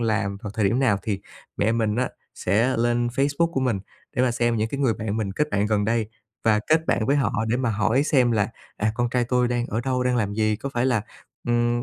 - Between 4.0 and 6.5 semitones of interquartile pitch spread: No, average, 2.8 semitones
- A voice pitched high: No, low, 120 Hz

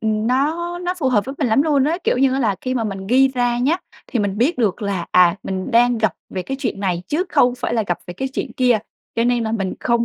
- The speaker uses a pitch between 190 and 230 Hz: No, high, 240 Hz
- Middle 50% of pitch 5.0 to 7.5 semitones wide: No, average, 4.6 semitones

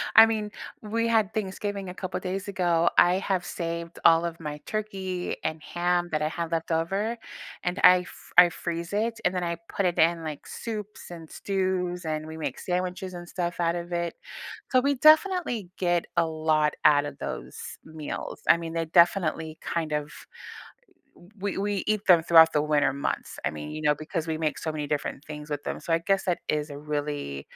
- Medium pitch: Yes, medium, 170 Hz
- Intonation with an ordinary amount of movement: Yes, average, 3.3 semitones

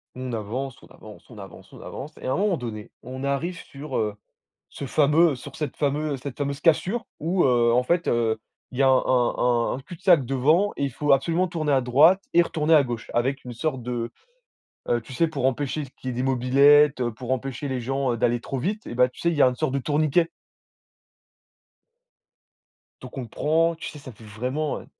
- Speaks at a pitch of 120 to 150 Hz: Yes, low, 135 Hz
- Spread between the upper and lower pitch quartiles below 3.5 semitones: No, average, 3.8 semitones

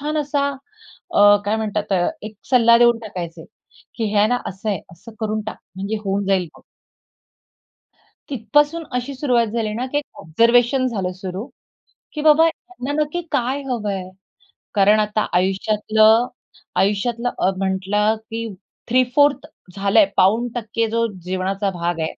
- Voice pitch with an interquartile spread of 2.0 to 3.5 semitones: No, average, 4.0 semitones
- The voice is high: Yes, high, 220 Hz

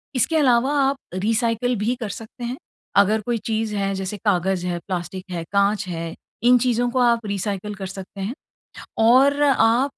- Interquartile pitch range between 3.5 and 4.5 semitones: Yes, average, 3.8 semitones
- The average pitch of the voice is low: No, high, 220 Hz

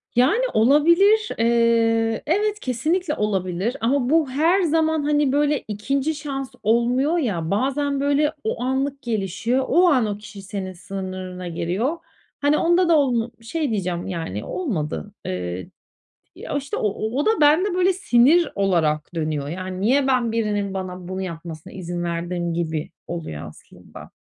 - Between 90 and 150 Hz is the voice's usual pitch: No, high, 230 Hz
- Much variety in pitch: Yes, wide, 7.8 semitones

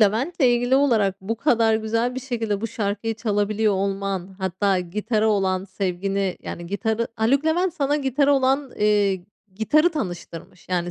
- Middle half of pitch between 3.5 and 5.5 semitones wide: Yes, average, 4.3 semitones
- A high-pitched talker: Yes, high, 215 Hz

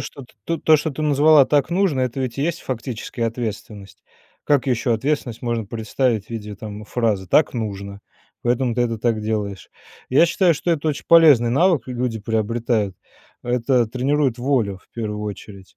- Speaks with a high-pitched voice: No, low, 120 Hz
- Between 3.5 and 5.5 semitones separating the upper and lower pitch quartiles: Yes, average, 4.3 semitones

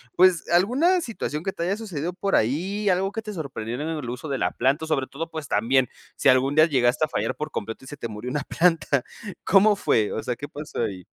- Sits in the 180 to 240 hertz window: No, medium, 150 Hz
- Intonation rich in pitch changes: Yes, wide, 6.0 semitones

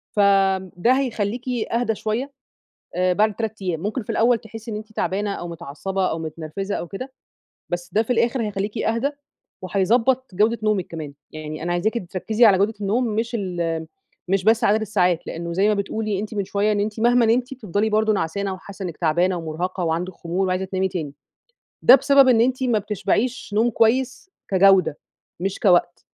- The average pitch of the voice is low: No, high, 205 Hz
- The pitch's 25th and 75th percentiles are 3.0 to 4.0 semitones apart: Yes, average, 3.7 semitones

